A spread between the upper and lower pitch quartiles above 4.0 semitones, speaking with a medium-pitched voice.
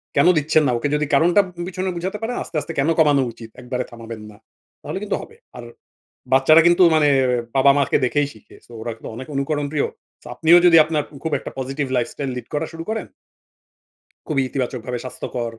Yes: average, 4.5 semitones; medium, 145 Hz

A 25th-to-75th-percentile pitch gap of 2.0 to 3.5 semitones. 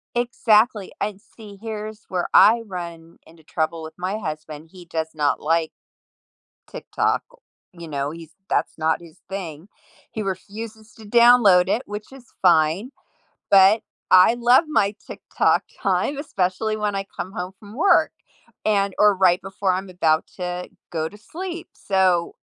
No: average, 4.3 semitones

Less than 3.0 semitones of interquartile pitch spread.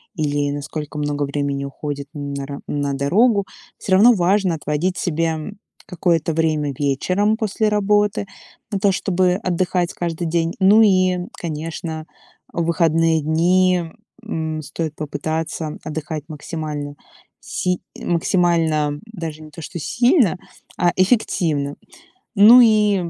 No: average, 3.7 semitones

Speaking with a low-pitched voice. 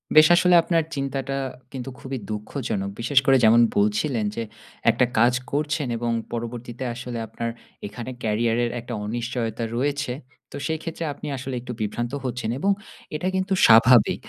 Yes: low, 125 Hz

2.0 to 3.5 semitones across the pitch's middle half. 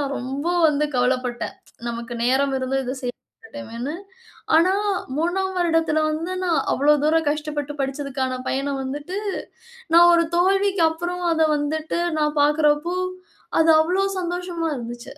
No: average, 4.0 semitones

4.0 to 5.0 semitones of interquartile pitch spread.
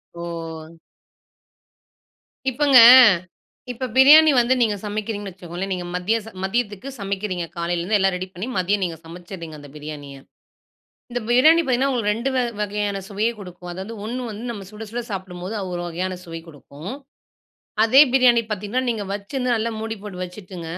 Yes: average, 4.7 semitones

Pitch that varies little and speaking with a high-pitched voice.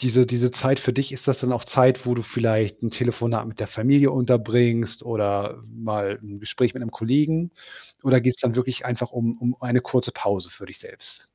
No: narrow, 2.2 semitones; low, 120 Hz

